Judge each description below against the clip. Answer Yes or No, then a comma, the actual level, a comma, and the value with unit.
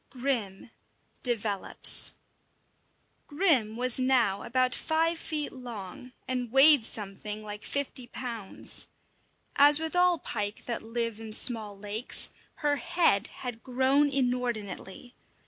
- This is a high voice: Yes, high, 245 Hz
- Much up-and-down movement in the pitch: No, average, 4.4 semitones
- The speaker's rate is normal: No, slow, 115 wpm